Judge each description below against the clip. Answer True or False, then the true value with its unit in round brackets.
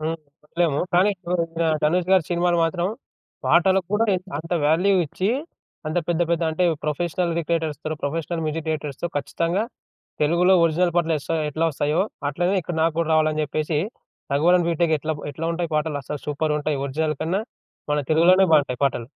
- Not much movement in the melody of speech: True (2.3 semitones)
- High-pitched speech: False (165 Hz)